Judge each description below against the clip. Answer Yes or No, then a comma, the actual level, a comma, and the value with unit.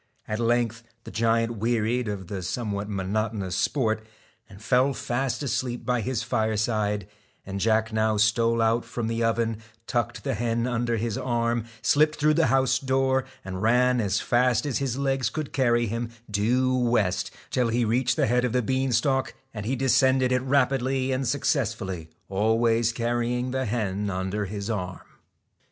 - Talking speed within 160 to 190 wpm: Yes, average, 165 wpm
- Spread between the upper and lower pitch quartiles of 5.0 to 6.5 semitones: No, average, 2.8 semitones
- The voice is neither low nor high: No, low, 115 Hz